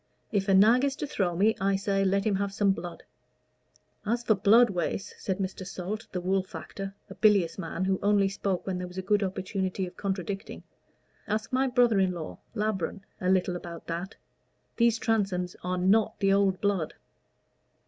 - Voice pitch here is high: Yes, high, 195 Hz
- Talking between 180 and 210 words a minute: Yes, average, 185 wpm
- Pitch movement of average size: No, narrow, 2.1 semitones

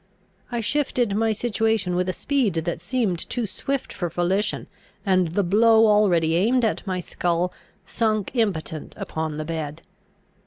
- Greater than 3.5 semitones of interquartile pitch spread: Yes, average, 4.5 semitones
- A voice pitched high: Yes, high, 195 Hz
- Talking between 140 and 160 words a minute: Yes, average, 150 wpm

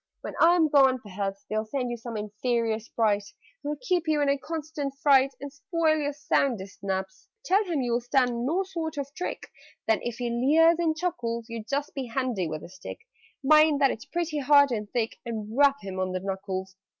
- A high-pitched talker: Yes, very high, 260 Hz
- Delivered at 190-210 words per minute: Yes, average, 200 wpm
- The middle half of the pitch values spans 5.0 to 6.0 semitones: Yes, average, 5.3 semitones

